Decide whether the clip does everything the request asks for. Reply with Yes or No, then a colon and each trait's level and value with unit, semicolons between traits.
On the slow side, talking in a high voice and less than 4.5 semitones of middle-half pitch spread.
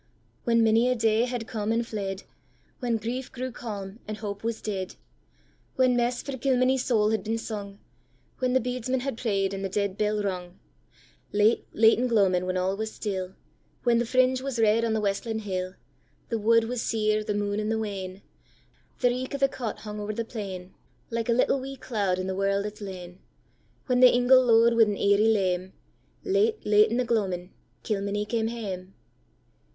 No: average, 170 wpm; high, 220 Hz; average, 3.3 semitones